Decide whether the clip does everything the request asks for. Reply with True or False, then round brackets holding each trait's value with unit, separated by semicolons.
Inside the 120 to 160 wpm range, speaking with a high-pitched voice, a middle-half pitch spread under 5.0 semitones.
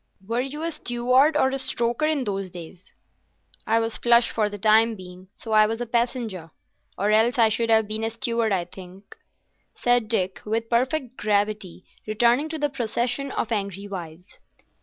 False (180 wpm; 225 Hz; 3.3 semitones)